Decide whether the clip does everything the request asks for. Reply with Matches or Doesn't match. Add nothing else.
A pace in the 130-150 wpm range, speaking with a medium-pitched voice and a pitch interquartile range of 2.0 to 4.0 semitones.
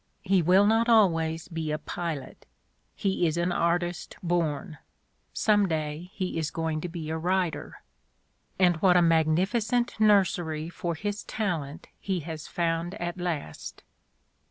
Matches